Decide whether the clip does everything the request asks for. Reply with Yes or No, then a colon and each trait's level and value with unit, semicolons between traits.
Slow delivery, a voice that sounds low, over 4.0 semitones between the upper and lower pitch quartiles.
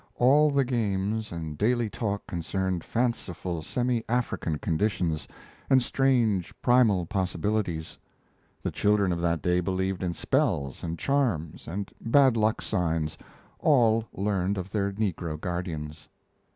Yes: slow, 125 wpm; low, 100 Hz; average, 5.2 semitones